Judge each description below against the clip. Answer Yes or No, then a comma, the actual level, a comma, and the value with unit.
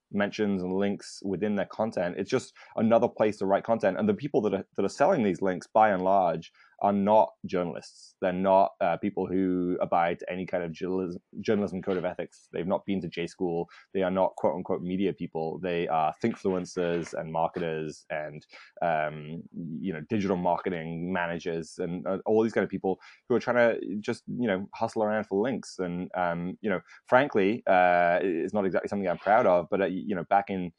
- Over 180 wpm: Yes, fast, 205 wpm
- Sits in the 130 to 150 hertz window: No, very low, 90 Hz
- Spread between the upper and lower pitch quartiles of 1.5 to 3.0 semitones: Yes, narrow, 2.4 semitones